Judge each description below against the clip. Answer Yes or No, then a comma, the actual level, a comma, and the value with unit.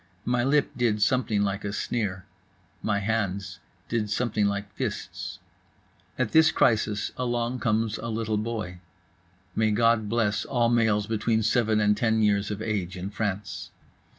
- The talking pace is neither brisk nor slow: Yes, average, 150 wpm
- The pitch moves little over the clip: Yes, narrow, 2.2 semitones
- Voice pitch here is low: Yes, low, 110 Hz